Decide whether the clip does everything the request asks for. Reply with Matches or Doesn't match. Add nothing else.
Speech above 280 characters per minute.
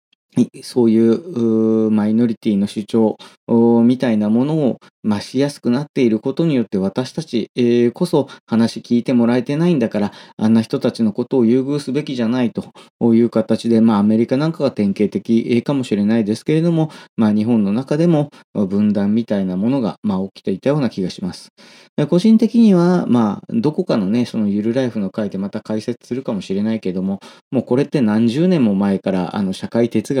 Matches